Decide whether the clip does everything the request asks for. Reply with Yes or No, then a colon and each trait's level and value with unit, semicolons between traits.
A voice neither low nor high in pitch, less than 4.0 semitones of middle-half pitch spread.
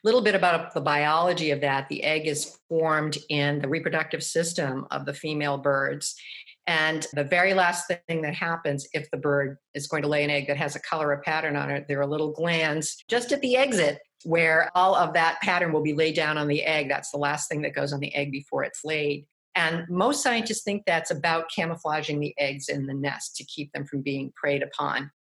Yes: medium, 155 Hz; narrow, 2.5 semitones